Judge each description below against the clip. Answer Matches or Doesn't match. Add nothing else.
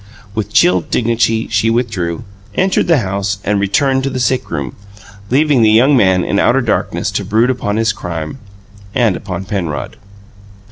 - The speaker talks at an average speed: Matches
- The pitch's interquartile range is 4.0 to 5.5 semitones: Matches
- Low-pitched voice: Matches